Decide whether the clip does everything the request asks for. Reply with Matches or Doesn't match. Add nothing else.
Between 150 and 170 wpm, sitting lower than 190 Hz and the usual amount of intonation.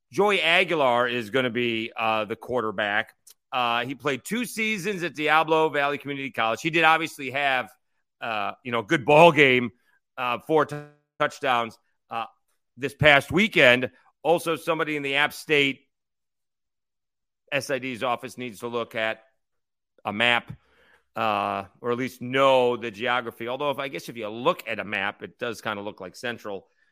Matches